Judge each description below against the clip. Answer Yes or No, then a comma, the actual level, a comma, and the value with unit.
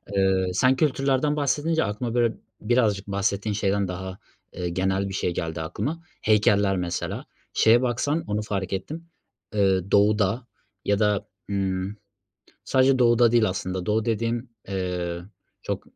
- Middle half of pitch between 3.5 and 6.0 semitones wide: Yes, average, 4.0 semitones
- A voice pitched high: No, low, 105 Hz